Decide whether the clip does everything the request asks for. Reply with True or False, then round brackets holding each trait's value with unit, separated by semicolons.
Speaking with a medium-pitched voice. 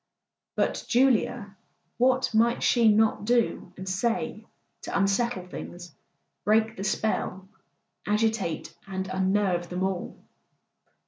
False (205 Hz)